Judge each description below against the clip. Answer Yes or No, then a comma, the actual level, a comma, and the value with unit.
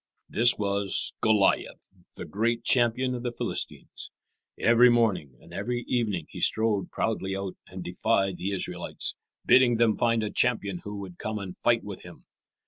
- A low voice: Yes, low, 110 Hz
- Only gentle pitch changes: No, average, 3.5 semitones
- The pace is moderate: Yes, average, 160 wpm